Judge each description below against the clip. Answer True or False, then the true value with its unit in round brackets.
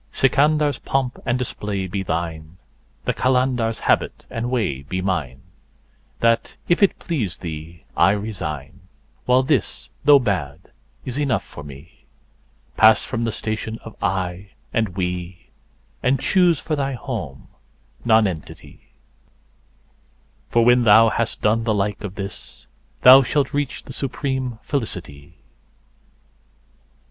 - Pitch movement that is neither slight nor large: False (6.3 semitones)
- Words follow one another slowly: True (120 wpm)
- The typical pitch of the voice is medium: False (110 Hz)